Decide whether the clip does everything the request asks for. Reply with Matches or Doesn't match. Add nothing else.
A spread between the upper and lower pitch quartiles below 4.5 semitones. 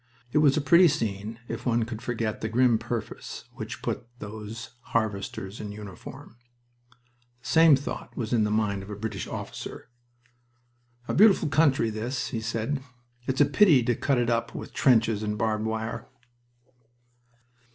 Matches